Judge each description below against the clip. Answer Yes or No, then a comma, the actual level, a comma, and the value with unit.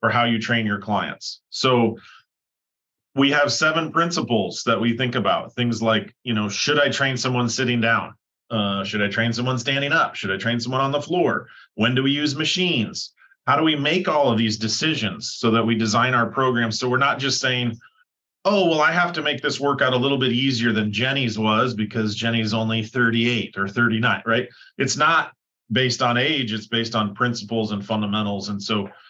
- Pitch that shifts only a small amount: No, average, 3.5 semitones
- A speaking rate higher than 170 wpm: Yes, average, 200 wpm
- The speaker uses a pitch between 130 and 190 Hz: No, low, 120 Hz